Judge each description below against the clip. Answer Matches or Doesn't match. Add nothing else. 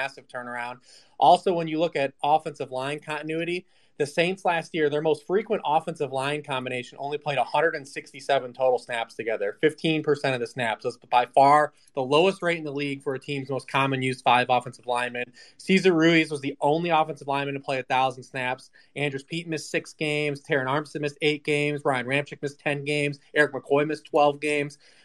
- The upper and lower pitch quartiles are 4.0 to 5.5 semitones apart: Doesn't match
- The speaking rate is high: Doesn't match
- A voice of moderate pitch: Matches